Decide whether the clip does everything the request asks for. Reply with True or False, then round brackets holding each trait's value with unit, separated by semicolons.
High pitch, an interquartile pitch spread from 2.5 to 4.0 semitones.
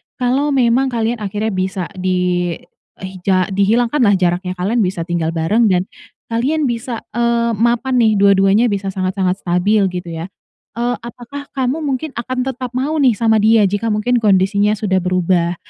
False (210 Hz; 4.4 semitones)